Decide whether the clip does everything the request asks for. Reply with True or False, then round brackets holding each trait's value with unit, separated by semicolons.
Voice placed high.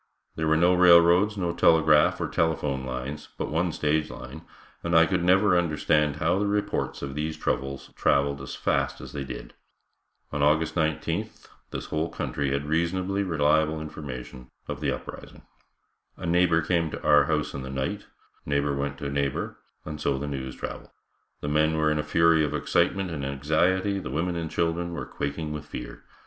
False (80 Hz)